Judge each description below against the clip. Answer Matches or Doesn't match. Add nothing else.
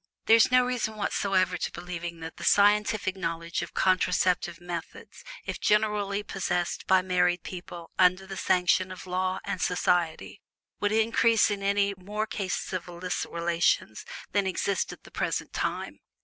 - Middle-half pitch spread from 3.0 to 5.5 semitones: Doesn't match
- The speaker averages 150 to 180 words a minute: Matches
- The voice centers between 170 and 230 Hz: Matches